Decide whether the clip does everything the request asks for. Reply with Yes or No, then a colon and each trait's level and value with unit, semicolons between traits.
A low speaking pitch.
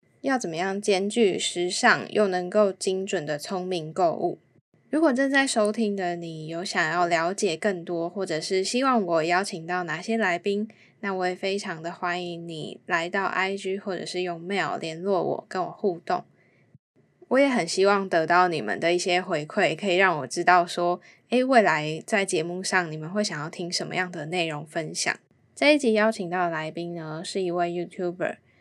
No: medium, 180 Hz